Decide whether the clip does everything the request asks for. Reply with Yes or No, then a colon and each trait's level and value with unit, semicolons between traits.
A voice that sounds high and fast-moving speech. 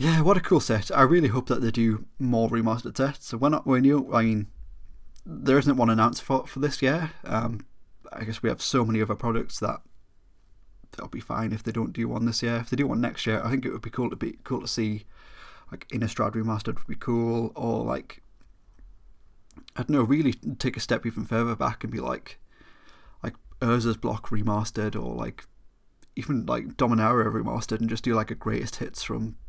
No: low, 115 Hz; fast, 215 wpm